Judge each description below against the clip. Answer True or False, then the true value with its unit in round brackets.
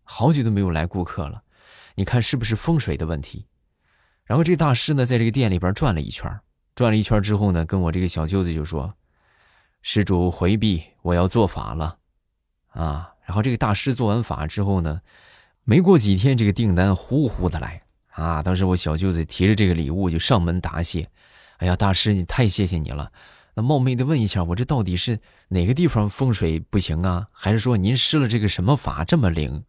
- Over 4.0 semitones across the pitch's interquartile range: True (5.2 semitones)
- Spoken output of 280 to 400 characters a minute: True (300 characters per minute)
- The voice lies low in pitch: True (95 Hz)